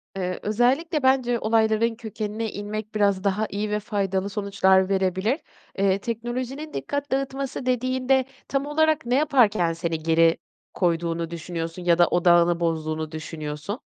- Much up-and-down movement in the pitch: Yes, wide, 6.2 semitones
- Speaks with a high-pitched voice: Yes, high, 205 Hz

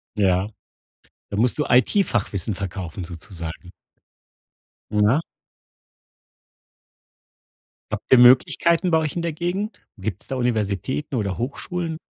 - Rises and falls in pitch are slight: No, wide, 8.2 semitones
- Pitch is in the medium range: No, low, 120 Hz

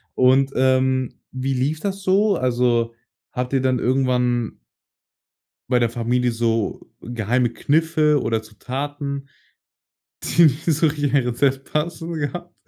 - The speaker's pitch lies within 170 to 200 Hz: No, low, 130 Hz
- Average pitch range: Yes, average, 3.3 semitones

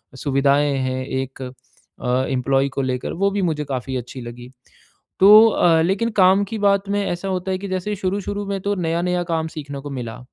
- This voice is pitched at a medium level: Yes, medium, 165 Hz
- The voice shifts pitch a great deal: Yes, wide, 6.6 semitones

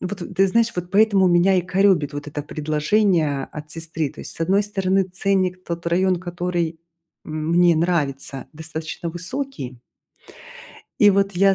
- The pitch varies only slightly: No, average, 3.4 semitones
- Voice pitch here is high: No, medium, 175 Hz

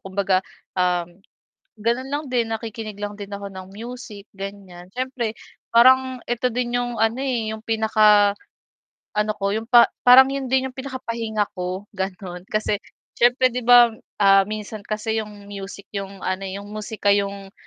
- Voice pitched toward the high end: Yes, high, 215 Hz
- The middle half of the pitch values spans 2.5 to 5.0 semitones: Yes, average, 3.3 semitones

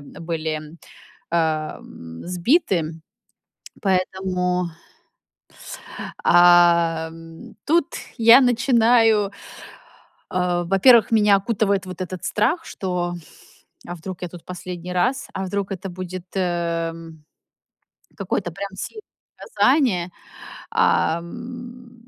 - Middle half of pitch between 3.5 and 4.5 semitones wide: Yes, average, 3.9 semitones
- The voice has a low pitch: No, medium, 180 Hz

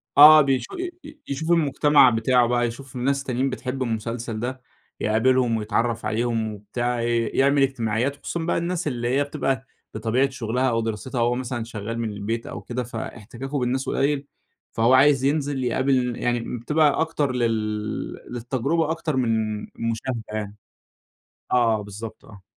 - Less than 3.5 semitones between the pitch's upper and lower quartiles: Yes, average, 3.1 semitones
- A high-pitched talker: No, low, 125 Hz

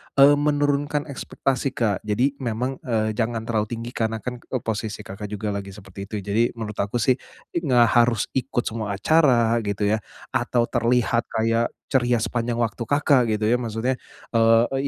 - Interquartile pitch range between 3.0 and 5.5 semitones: No, narrow, 2.6 semitones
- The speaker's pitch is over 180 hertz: No, low, 115 Hz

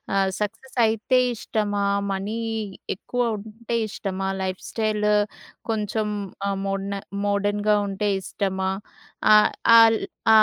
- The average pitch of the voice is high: Yes, high, 210 Hz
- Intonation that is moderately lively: No, narrow, 2.0 semitones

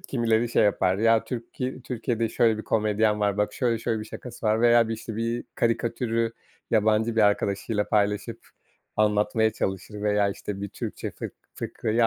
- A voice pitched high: No, low, 110 Hz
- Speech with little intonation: Yes, narrow, 1.8 semitones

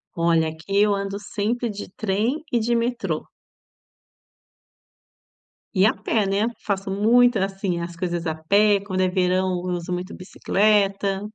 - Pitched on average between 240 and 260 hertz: No, high, 195 Hz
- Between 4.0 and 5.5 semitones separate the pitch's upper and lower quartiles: No, narrow, 2.5 semitones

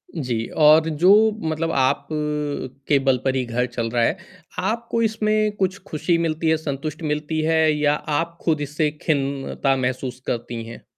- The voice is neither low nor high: Yes, medium, 150 Hz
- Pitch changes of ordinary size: Yes, average, 3.7 semitones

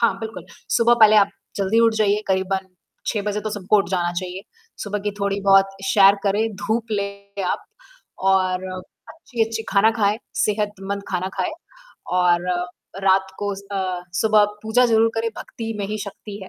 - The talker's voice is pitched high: Yes, high, 200 Hz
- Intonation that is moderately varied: No, narrow, 2.2 semitones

